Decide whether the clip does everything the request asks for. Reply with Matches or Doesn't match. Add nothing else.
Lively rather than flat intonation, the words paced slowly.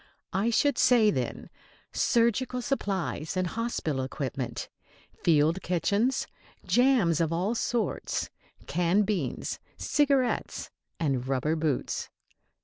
Matches